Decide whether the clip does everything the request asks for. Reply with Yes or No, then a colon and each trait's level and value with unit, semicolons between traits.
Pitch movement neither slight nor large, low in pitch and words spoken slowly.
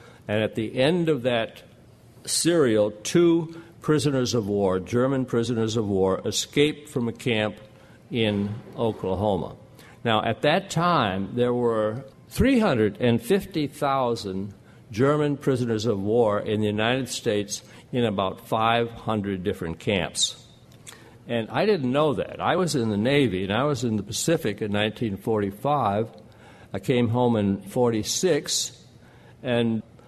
Yes: average, 3.9 semitones; low, 115 Hz; slow, 130 wpm